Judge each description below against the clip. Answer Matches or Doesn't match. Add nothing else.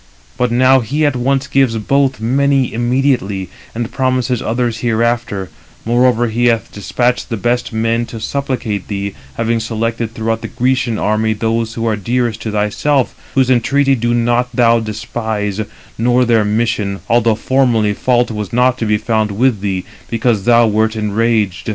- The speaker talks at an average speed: Matches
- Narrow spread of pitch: Matches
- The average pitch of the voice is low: Matches